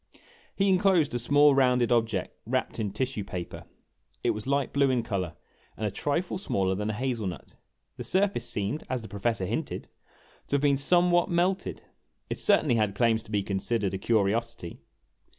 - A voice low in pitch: Yes, low, 120 Hz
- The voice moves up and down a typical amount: No, wide, 5.8 semitones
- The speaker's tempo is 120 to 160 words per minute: No, average, 180 wpm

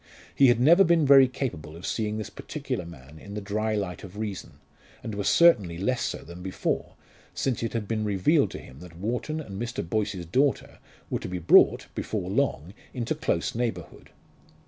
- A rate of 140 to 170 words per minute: No, average, 190 wpm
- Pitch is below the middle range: Yes, low, 105 Hz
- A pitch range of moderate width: No, wide, 5.8 semitones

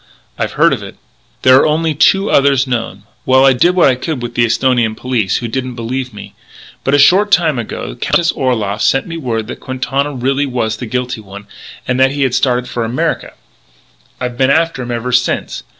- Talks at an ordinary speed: No, fast, 210 wpm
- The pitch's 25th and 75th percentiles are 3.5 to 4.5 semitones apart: No, narrow, 2.6 semitones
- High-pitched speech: No, low, 130 Hz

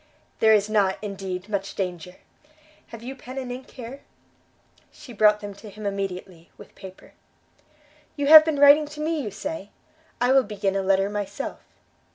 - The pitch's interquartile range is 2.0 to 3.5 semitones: No, average, 5.1 semitones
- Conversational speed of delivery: Yes, average, 170 wpm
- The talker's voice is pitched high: Yes, high, 210 Hz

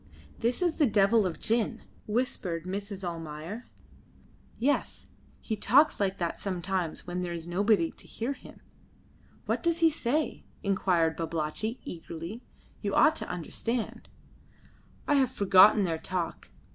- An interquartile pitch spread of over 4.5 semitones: Yes, average, 5.3 semitones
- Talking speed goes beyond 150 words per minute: No, slow, 135 wpm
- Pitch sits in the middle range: No, high, 195 Hz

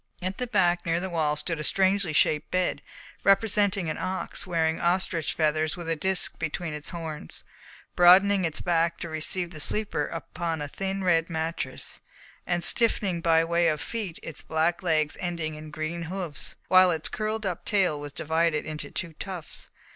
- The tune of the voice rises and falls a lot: No, average, 2.8 semitones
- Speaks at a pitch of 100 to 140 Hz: No, medium, 170 Hz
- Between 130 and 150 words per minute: No, average, 175 wpm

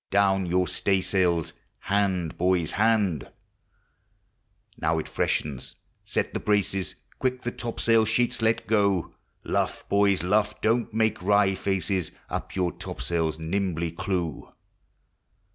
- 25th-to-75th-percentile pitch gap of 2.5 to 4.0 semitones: Yes, average, 3.3 semitones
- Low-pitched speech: Yes, very low, 95 Hz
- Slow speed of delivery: Yes, slow, 120 wpm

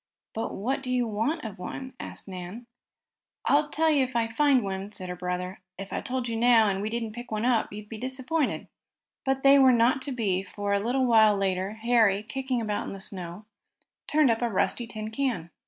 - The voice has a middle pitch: No, high, 225 Hz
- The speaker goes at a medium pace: No, fast, 210 wpm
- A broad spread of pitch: No, average, 4.4 semitones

